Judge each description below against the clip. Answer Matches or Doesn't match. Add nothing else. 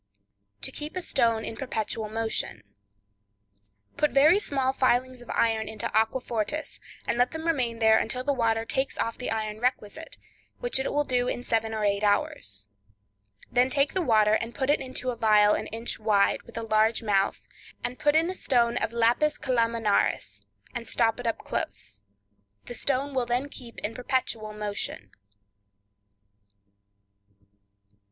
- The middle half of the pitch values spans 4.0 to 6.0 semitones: Doesn't match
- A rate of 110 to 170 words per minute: Matches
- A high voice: Matches